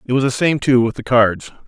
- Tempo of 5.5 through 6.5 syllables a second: Yes, 5.6 syllables/s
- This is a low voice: Yes, low, 125 Hz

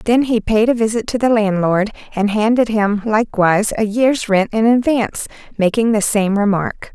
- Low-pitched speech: No, high, 215 Hz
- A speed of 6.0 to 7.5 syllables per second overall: No, 4.9 syllables/s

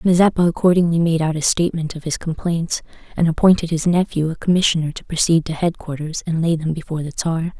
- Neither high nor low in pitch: Yes, medium, 165 Hz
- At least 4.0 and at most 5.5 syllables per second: No, 6.2 syllables/s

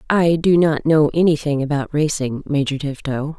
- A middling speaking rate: Yes, average, 160 wpm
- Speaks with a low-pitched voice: No, medium, 150 Hz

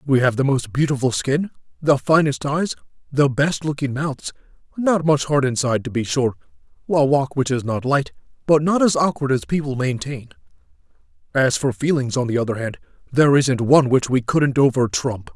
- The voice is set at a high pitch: No, low, 135 Hz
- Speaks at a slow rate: No, average, 175 wpm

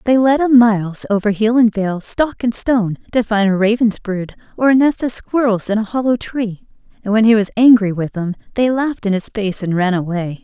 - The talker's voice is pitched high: Yes, high, 220 Hz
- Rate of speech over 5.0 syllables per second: Yes, 5.3 syllables/s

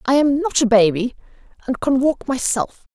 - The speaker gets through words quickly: No, average, 185 wpm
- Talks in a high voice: Yes, very high, 255 Hz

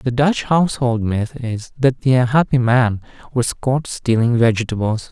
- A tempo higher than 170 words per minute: No, average, 155 wpm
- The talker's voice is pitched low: Yes, low, 125 Hz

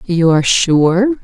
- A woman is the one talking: Yes, female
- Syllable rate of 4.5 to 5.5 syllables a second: No, 3.9 syllables/s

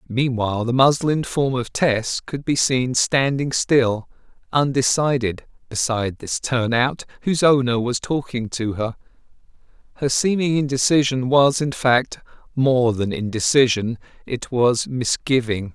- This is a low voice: Yes, low, 130 Hz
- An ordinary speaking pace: No, slow, 130 wpm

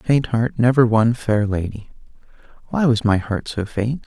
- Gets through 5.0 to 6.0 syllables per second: No, 4.4 syllables/s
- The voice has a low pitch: Yes, low, 115 Hz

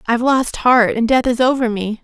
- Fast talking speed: Yes, fast, 235 wpm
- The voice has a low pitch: No, high, 240 Hz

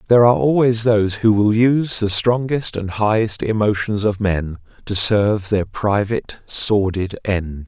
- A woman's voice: No, male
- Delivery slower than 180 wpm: Yes, average, 155 wpm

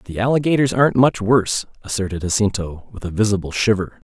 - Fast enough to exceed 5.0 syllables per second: Yes, 6.1 syllables/s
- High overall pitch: No, low, 105 Hz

